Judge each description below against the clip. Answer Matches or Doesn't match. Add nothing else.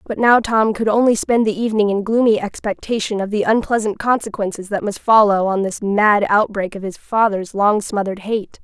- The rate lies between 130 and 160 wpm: Doesn't match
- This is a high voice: Matches